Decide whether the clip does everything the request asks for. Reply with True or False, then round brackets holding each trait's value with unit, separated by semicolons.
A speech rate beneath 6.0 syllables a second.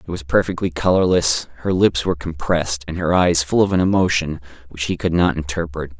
True (5.7 syllables/s)